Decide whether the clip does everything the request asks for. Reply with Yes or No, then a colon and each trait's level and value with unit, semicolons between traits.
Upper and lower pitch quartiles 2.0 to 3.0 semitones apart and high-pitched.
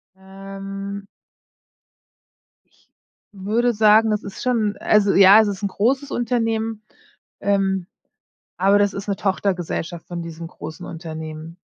Yes: narrow, 2.4 semitones; high, 200 Hz